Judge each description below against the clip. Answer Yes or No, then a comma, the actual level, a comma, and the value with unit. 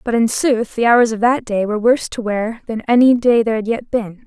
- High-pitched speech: Yes, high, 230 Hz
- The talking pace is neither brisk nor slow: No, fast, 265 wpm